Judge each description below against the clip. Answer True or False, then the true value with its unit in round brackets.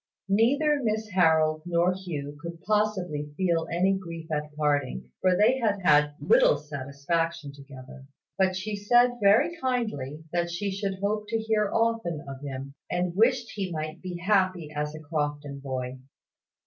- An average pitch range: False (5.9 semitones)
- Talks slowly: False (155 wpm)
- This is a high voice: False (175 Hz)